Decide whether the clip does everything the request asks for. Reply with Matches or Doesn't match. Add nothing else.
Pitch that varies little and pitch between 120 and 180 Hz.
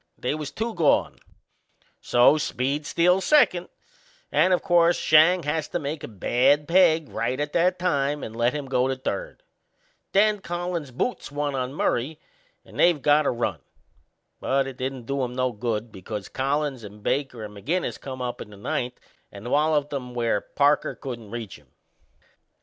Doesn't match